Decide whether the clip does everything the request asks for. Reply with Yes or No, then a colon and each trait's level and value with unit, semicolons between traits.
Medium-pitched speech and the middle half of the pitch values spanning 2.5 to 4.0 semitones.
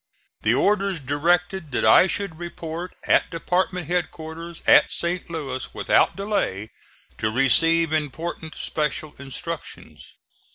Yes: medium, 165 Hz; average, 3.1 semitones